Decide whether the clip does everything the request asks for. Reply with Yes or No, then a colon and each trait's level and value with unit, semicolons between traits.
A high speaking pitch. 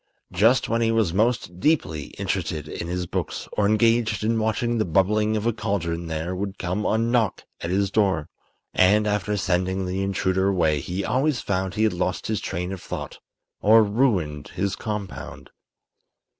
No: low, 100 Hz